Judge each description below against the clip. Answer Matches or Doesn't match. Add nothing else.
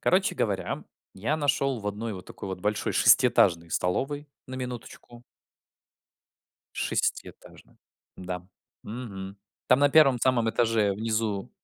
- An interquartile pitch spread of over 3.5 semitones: Matches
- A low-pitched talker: Matches